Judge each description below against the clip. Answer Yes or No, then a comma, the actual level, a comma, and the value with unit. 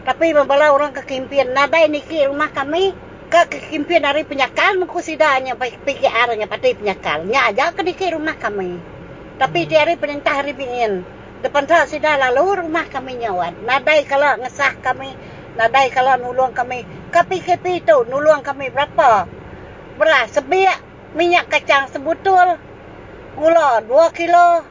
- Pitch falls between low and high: No, very high, 290 Hz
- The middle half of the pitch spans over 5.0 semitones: No, average, 4.2 semitones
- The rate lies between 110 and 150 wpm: Yes, average, 140 wpm